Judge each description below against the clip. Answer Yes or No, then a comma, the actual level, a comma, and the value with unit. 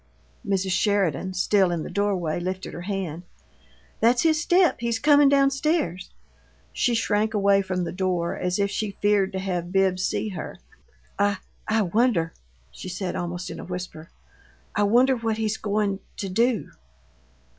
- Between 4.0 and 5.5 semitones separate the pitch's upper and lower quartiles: No, average, 3.4 semitones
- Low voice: No, high, 195 Hz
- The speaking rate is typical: Yes, average, 165 wpm